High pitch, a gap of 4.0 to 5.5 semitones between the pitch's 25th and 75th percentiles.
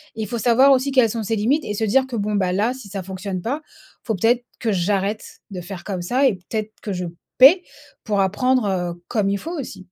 Yes: high, 215 Hz; average, 4.5 semitones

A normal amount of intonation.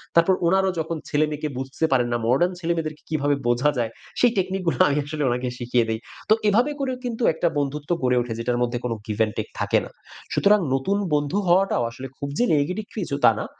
No: wide, 6.7 semitones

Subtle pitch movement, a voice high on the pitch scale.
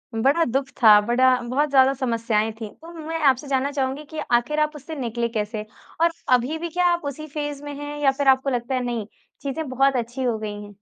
No: average, 3.5 semitones; very high, 265 Hz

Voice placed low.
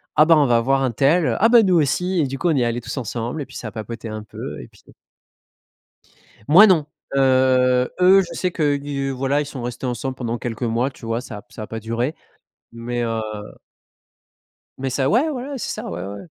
Yes: low, 130 Hz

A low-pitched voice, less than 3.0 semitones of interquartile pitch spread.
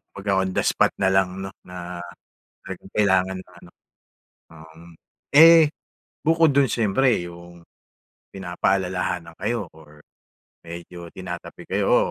Yes: very low, 95 Hz; narrow, 2.5 semitones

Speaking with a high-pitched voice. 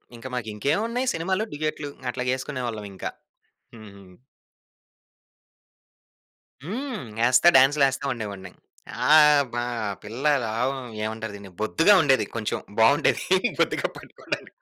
No: low, 130 Hz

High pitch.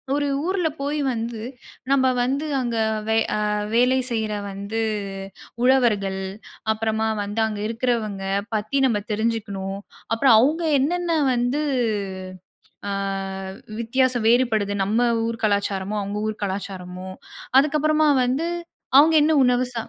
Yes: high, 230 Hz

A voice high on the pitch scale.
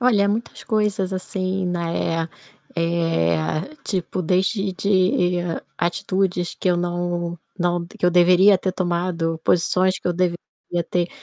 No: medium, 180 Hz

